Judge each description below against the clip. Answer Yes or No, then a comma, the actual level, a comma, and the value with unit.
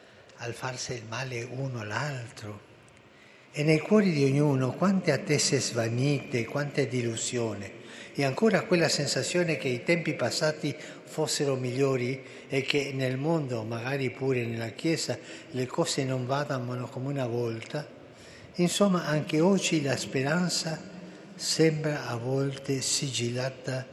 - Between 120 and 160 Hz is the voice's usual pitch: Yes, low, 135 Hz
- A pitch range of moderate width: Yes, average, 3.8 semitones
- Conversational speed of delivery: Yes, average, 125 wpm